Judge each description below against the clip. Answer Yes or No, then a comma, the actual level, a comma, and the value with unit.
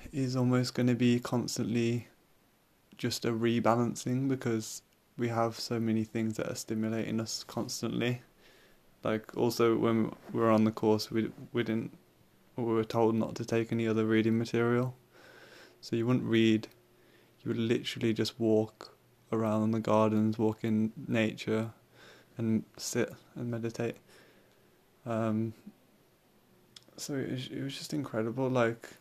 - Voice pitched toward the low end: Yes, low, 115 Hz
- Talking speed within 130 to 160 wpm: Yes, average, 145 wpm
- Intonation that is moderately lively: No, narrow, 1.3 semitones